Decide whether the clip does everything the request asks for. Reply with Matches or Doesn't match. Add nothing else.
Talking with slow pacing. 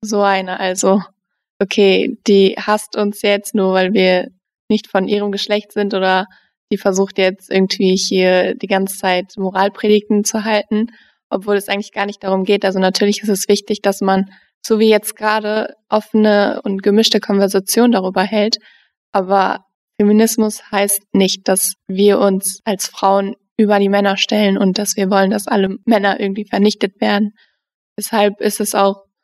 Doesn't match